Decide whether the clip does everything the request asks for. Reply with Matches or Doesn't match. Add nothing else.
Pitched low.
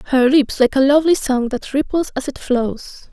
Doesn't match